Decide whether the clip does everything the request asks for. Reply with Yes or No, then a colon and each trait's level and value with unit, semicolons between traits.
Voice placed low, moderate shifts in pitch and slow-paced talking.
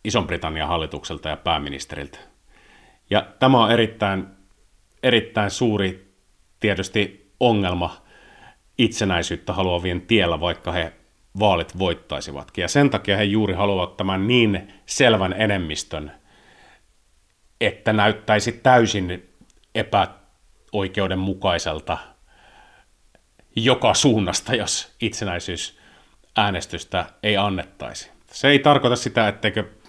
Yes: low, 100 Hz; average, 3.4 semitones; slow, 90 wpm